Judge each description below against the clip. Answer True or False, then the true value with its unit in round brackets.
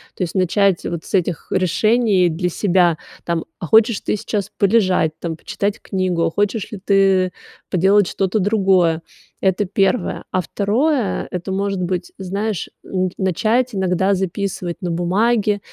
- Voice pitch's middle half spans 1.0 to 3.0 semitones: True (2.4 semitones)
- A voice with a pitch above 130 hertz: True (190 Hz)